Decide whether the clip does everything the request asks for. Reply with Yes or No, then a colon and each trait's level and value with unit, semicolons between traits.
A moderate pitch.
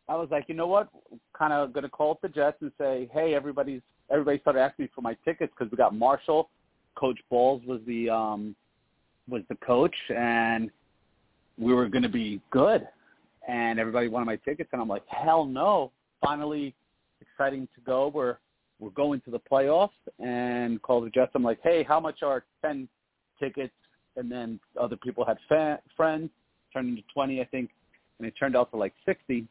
No: low, 130 Hz